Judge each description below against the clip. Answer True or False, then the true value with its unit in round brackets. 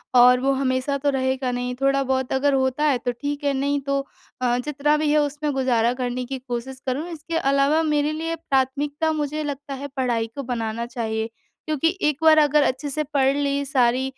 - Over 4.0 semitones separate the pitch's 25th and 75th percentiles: False (2.5 semitones)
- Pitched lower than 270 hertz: False (275 Hz)